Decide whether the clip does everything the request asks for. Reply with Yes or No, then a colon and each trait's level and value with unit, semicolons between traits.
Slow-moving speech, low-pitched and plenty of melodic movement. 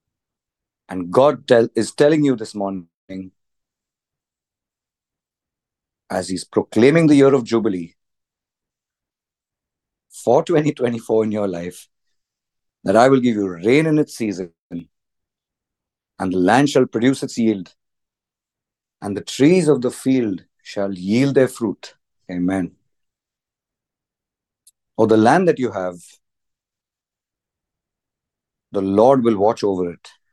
Yes: slow, 120 wpm; low, 110 Hz; wide, 5.9 semitones